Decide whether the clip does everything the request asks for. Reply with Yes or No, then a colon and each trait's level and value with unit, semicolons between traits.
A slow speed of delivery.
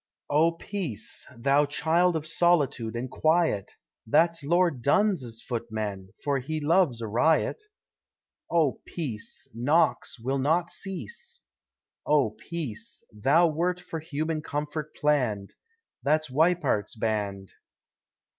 Yes: slow, 110 wpm